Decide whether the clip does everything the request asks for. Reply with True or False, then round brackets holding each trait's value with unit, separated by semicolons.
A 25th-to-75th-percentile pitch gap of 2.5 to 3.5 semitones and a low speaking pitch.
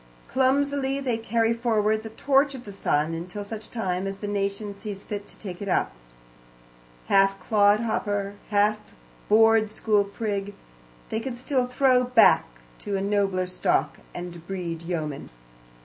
False (2.9 semitones; 205 Hz)